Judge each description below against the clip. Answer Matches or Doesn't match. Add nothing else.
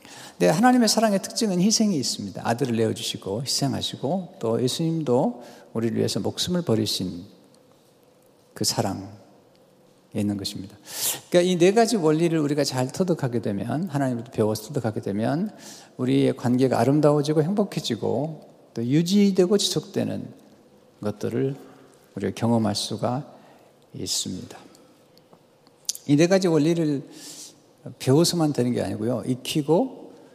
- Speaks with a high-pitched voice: Doesn't match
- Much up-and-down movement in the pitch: Matches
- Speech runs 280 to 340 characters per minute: Matches